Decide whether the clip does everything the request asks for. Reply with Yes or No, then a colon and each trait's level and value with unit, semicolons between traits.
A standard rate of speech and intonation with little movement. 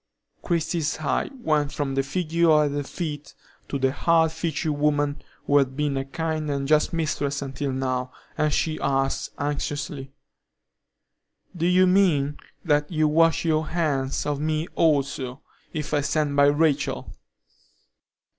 Yes: average, 145 wpm; narrow, 2.3 semitones